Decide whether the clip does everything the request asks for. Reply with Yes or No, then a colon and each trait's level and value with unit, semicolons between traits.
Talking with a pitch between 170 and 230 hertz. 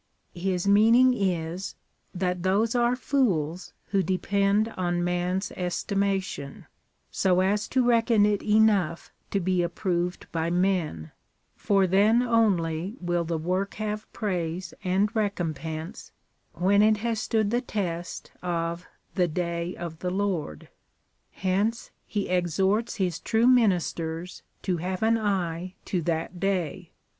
Yes: medium, 185 Hz